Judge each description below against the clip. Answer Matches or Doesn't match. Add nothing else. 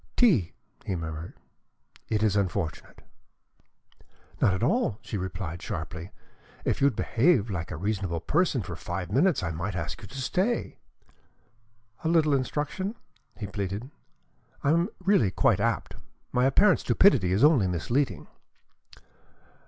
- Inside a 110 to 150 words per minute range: Matches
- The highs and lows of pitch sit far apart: Matches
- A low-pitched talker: Matches